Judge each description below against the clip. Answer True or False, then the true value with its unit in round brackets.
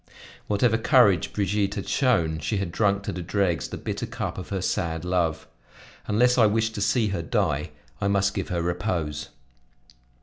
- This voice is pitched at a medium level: False (100 Hz)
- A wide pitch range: False (3.6 semitones)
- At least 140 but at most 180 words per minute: True (175 wpm)